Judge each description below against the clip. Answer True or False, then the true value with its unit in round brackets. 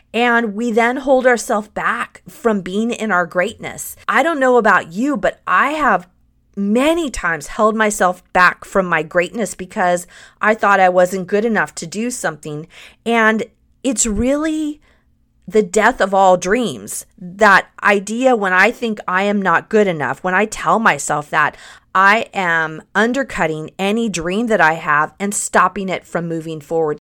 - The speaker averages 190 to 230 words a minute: False (165 wpm)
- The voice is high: True (200 Hz)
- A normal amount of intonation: True (4.1 semitones)